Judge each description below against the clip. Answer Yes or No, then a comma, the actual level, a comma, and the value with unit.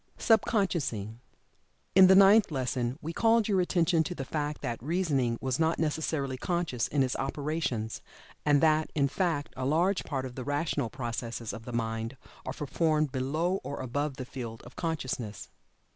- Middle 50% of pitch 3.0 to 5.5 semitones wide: Yes, average, 4.7 semitones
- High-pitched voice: No, medium, 145 Hz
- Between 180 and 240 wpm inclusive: No, average, 170 wpm